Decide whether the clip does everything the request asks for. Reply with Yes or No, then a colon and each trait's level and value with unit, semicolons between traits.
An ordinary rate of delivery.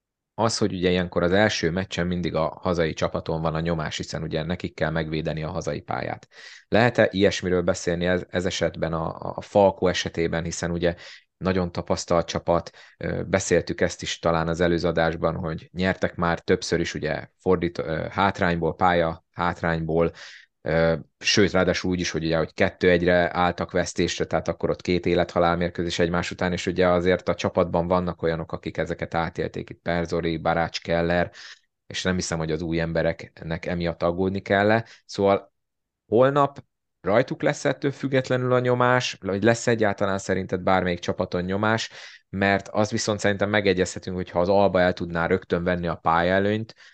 No: fast, 165 wpm